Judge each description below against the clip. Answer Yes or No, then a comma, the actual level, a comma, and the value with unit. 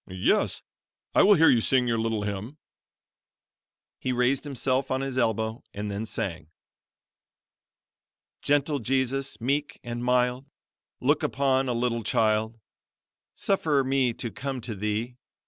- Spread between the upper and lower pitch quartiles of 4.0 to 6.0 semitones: No, average, 3.4 semitones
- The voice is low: Yes, low, 125 Hz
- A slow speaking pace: Yes, slow, 130 wpm